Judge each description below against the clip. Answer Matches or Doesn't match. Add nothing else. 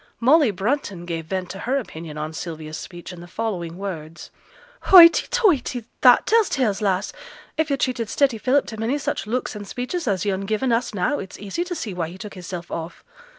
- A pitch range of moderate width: Doesn't match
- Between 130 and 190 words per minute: Doesn't match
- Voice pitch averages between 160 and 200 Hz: Doesn't match